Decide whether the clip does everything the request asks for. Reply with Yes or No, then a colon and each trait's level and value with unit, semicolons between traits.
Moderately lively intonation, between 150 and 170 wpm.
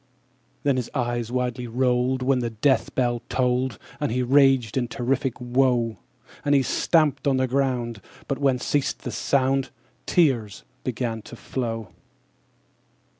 No: narrow, 2.0 semitones; average, 160 wpm